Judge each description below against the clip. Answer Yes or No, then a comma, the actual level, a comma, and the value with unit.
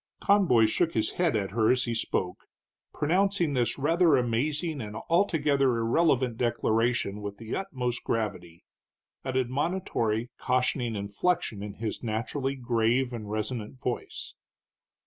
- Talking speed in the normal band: No, slow, 125 wpm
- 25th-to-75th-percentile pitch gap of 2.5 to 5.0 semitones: Yes, average, 4.7 semitones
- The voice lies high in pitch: No, low, 120 Hz